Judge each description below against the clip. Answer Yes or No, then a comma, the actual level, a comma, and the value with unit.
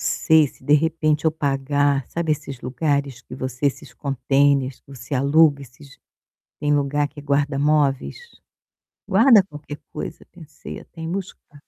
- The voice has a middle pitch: Yes, medium, 145 Hz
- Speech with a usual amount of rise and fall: No, narrow, 2.0 semitones